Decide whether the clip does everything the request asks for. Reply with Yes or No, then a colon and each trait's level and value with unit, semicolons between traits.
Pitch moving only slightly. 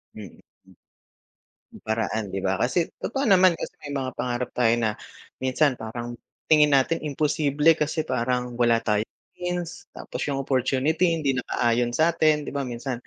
No: average, 4.6 semitones